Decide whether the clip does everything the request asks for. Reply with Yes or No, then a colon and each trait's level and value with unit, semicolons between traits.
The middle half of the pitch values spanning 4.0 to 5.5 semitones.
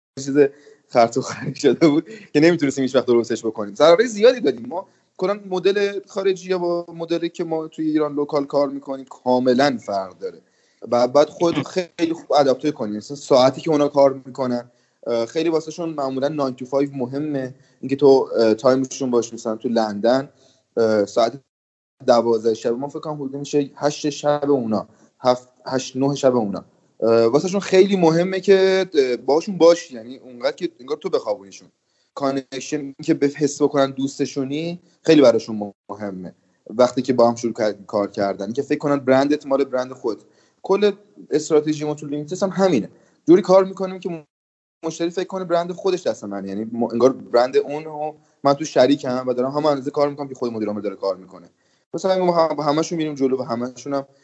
Yes: average, 4.5 semitones